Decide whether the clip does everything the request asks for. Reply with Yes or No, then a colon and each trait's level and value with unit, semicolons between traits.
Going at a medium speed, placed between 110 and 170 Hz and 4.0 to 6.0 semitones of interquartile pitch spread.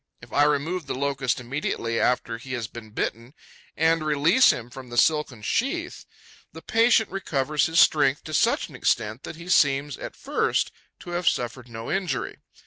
Yes: average, 175 wpm; medium, 140 Hz; average, 4.9 semitones